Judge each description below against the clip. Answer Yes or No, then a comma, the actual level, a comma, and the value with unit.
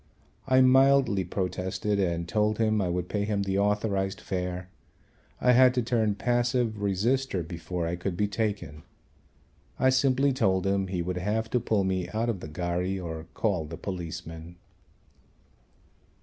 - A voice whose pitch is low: Yes, low, 100 Hz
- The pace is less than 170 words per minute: Yes, average, 155 wpm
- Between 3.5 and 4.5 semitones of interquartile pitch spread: Yes, average, 3.9 semitones